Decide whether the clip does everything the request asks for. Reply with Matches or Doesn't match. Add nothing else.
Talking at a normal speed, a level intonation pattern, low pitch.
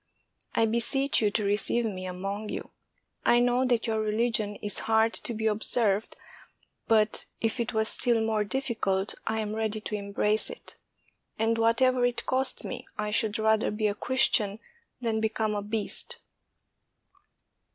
Doesn't match